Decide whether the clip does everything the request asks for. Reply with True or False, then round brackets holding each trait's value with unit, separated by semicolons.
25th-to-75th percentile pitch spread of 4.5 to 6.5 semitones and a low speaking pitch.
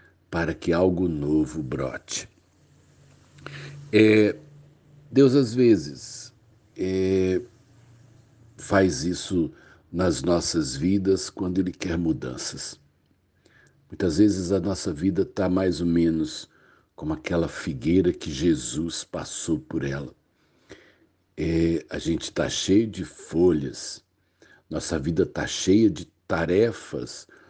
True (5.3 semitones; 95 Hz)